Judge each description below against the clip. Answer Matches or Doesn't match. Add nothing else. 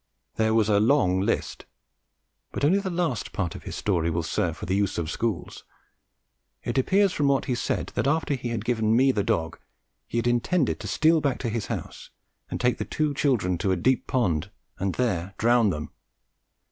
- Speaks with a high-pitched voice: Doesn't match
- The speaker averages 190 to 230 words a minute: Matches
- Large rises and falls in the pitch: Matches